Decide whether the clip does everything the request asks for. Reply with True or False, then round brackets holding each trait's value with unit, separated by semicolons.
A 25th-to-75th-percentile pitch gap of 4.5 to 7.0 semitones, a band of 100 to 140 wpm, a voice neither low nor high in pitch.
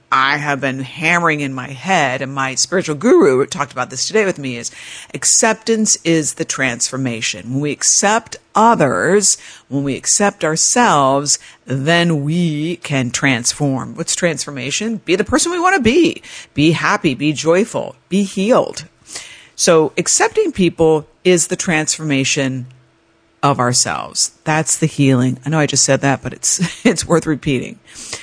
False (5.4 semitones; 150 wpm; 155 Hz)